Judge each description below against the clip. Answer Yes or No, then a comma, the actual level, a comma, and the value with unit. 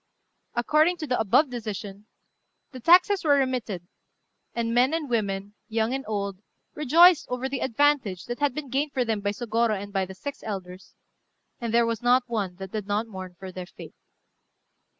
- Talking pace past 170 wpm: Yes, average, 185 wpm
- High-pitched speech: Yes, high, 230 Hz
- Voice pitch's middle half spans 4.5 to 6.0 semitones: Yes, average, 5.1 semitones